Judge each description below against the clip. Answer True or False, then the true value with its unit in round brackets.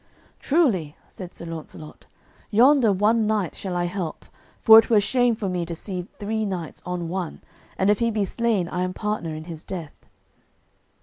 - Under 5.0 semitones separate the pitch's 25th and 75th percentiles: True (4.0 semitones)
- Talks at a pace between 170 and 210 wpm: True (180 wpm)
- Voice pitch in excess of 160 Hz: True (190 Hz)